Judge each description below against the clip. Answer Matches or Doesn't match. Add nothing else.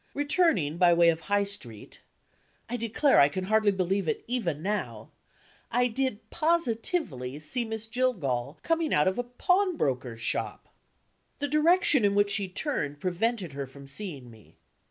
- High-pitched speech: Matches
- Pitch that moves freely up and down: Matches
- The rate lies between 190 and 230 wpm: Doesn't match